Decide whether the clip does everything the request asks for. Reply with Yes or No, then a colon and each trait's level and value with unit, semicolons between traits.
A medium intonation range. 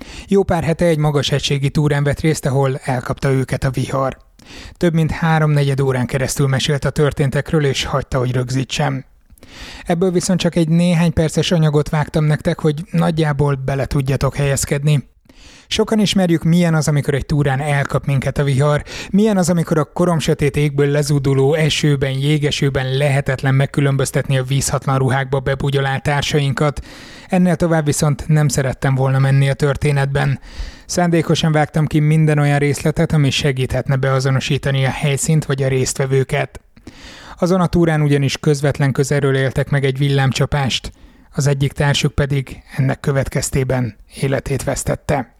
No: narrow, 2.3 semitones